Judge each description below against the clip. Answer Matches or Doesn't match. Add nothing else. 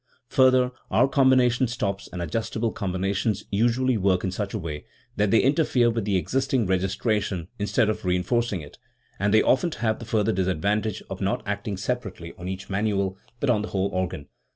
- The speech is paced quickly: Doesn't match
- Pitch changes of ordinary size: Matches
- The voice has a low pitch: Matches